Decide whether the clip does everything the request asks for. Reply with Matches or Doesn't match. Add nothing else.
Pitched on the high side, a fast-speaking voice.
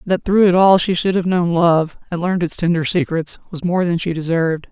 Doesn't match